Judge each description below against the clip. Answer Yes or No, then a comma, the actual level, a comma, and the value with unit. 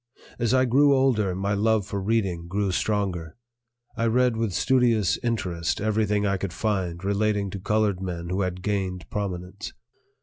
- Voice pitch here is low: Yes, low, 100 Hz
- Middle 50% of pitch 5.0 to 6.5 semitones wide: No, average, 3.2 semitones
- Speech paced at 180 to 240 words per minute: No, average, 160 wpm